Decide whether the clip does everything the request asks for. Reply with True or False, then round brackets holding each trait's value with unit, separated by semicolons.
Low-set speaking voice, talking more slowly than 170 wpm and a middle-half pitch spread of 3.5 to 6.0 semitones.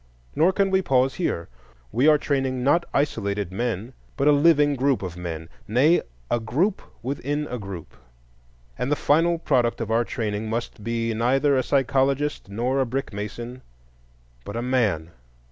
True (125 Hz; 155 wpm; 4.4 semitones)